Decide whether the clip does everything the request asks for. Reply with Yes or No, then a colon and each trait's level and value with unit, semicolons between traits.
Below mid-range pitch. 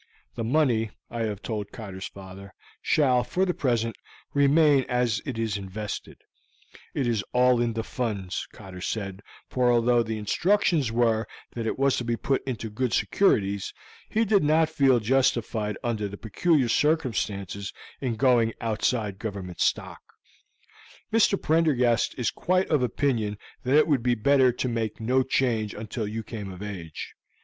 Yes: low, 115 Hz